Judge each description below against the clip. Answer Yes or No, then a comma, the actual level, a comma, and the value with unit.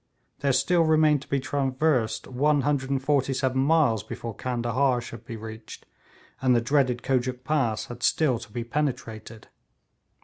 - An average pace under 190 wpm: Yes, slow, 135 wpm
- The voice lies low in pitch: Yes, low, 130 Hz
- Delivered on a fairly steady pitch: No, average, 3.2 semitones